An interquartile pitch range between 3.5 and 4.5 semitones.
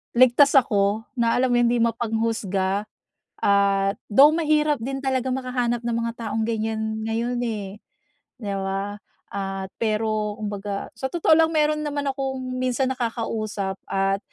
Yes: average, 4.0 semitones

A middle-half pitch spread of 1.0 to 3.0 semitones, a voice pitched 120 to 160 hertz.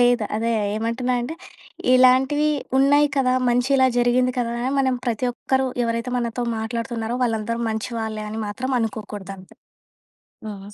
No: narrow, 2.5 semitones; high, 240 Hz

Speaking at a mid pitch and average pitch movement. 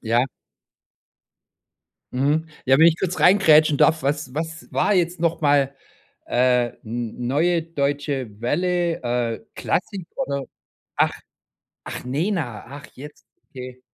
Yes: medium, 145 Hz; average, 4.7 semitones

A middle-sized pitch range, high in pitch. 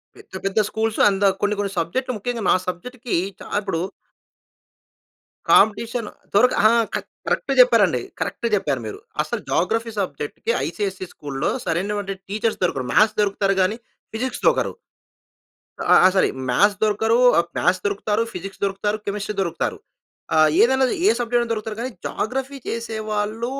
Yes: average, 3.1 semitones; high, 210 Hz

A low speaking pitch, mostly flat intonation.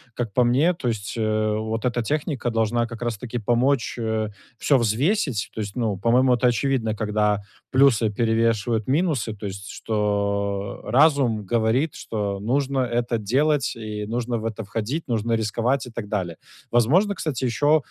No: low, 115 Hz; average, 3.2 semitones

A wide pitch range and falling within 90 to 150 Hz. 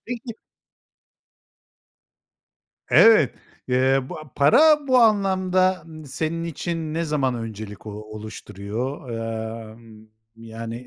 Yes: wide, 8.3 semitones; medium, 140 Hz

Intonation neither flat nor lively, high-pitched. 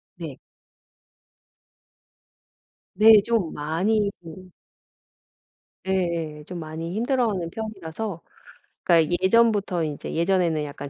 No: average, 4.6 semitones; medium, 180 Hz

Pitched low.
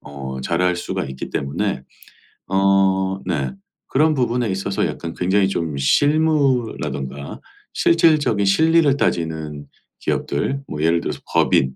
Yes: very low, 95 Hz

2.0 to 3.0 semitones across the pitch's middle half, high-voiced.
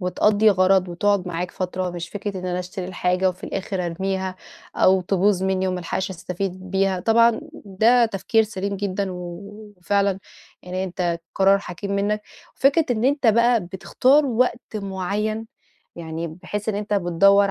Yes: narrow, 2.4 semitones; high, 195 Hz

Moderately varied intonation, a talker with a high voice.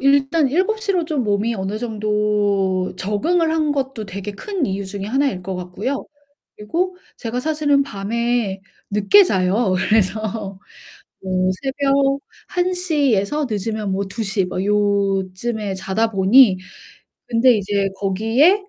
No: wide, 5.9 semitones; high, 215 Hz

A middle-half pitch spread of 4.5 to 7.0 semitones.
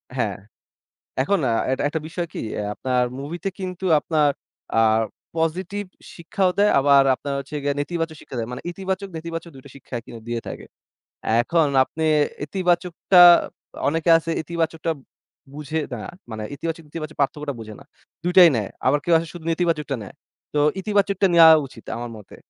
No: average, 3.9 semitones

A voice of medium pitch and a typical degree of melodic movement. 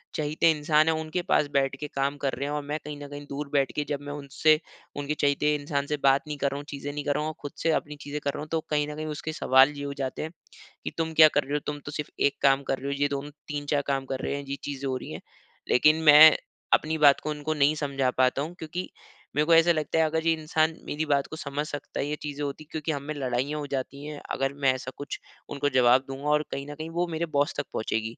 No: medium, 145 Hz; narrow, 1.6 semitones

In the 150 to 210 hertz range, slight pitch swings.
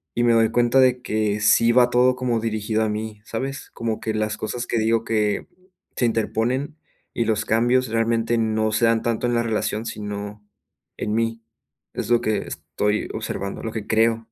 No: low, 115 Hz; narrow, 1.6 semitones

